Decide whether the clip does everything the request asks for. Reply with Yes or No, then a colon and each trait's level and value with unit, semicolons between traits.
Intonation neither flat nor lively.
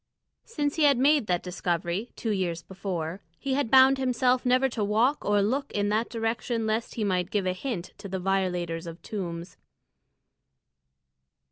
No: wide, 5.7 semitones